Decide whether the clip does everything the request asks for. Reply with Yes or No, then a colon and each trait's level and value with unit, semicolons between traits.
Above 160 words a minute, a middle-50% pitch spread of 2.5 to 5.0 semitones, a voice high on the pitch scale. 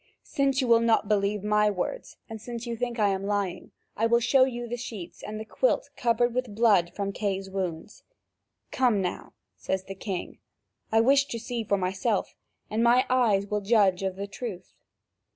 Yes: average, 190 wpm; average, 3.4 semitones; high, 215 Hz